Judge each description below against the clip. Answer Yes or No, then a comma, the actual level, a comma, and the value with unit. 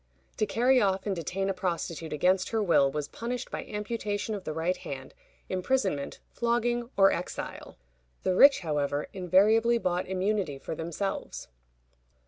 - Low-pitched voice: No, high, 190 Hz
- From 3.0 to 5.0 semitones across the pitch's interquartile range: Yes, average, 4.7 semitones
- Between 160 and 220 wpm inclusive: No, average, 145 wpm